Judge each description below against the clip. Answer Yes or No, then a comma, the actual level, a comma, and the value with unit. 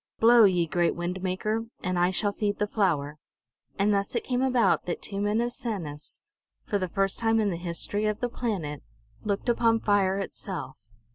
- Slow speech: No, average, 190 wpm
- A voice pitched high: Yes, high, 200 Hz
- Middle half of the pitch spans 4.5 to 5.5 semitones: No, average, 3.7 semitones